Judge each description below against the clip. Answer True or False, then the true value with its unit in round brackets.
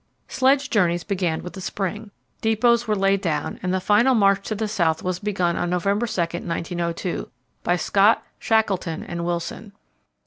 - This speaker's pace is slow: False (165 wpm)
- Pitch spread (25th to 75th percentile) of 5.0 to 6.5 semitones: False (3.6 semitones)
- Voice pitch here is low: False (195 Hz)